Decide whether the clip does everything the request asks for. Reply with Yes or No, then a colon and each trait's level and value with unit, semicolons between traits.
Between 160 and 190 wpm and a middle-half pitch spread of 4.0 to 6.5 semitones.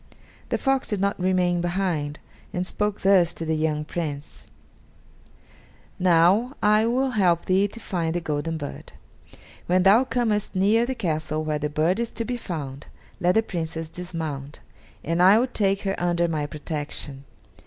Yes: average, 165 wpm; average, 4.5 semitones